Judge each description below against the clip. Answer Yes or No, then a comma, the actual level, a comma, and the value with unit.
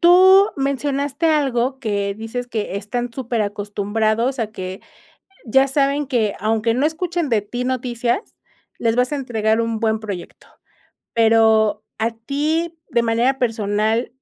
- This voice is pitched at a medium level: No, high, 235 Hz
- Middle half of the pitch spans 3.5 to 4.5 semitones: Yes, average, 3.8 semitones